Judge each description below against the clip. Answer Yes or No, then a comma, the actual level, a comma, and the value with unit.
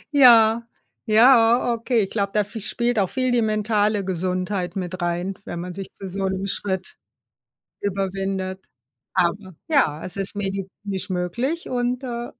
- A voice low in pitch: No, high, 200 Hz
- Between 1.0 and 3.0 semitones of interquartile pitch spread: No, average, 3.6 semitones